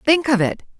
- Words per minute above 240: No, fast, 225 wpm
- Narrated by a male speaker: No, female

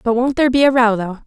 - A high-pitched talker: Yes, high, 240 Hz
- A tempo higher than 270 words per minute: Yes, fast, 330 wpm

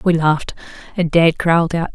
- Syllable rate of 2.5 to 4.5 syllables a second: No, 5.7 syllables/s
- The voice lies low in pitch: No, medium, 165 Hz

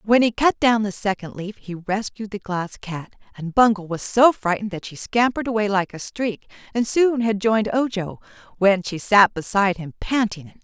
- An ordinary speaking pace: No, fast, 210 wpm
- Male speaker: No, female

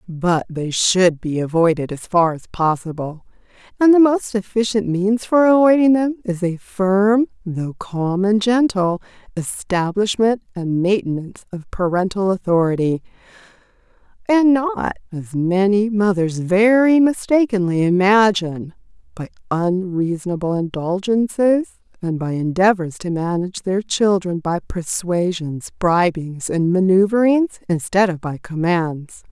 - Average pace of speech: No, slow, 115 wpm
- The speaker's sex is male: No, female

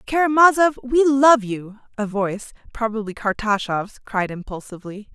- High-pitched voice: Yes, high, 230 Hz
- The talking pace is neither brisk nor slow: No, slow, 115 wpm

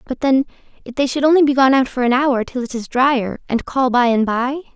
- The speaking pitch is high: Yes, very high, 255 Hz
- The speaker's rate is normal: No, fast, 265 wpm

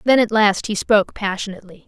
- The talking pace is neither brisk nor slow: Yes, average, 190 wpm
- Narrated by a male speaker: No, female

